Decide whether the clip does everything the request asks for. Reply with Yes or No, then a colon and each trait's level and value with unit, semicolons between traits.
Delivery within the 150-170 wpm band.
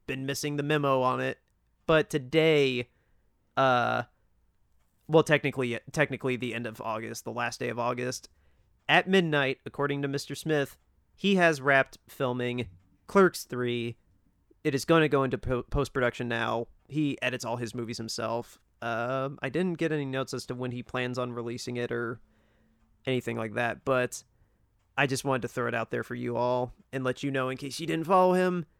No: average, 185 wpm